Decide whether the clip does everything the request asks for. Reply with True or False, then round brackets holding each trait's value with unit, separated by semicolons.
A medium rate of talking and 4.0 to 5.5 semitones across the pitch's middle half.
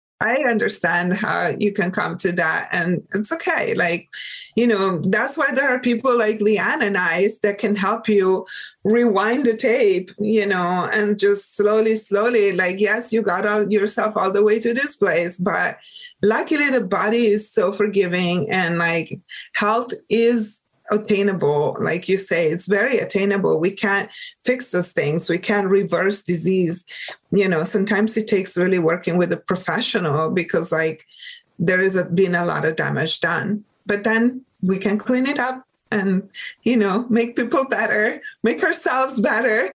False (170 wpm; 3.6 semitones)